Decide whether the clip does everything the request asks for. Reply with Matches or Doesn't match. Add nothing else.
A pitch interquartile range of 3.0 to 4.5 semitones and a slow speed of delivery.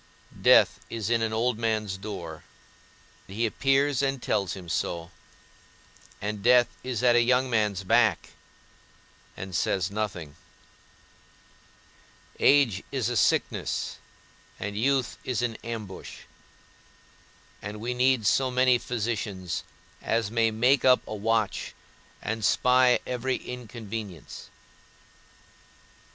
Matches